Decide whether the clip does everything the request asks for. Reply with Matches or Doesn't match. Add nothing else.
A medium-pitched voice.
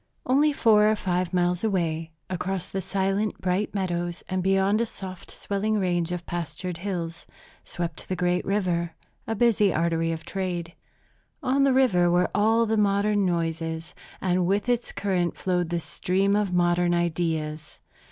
Matches